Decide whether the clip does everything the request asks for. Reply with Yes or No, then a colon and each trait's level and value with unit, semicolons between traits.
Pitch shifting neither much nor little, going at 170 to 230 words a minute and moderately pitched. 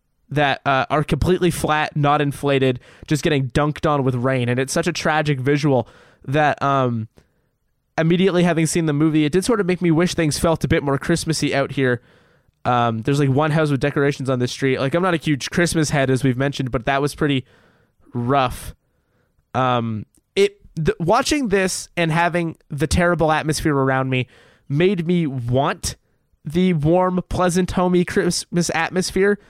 Yes: average, 4.3 semitones; average, 175 wpm; medium, 150 Hz